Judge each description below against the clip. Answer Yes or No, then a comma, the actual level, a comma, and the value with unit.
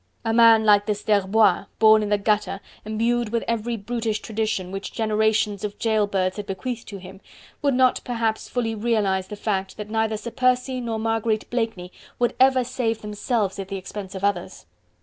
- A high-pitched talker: Yes, high, 220 Hz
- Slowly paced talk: No, average, 185 wpm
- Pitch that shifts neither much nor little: No, narrow, 2.3 semitones